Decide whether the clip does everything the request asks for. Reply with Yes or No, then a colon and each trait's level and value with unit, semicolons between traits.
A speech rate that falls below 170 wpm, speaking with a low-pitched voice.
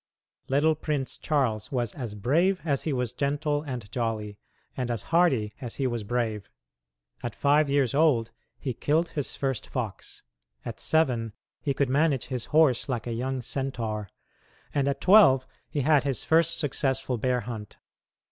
Yes: average, 160 wpm; low, 130 Hz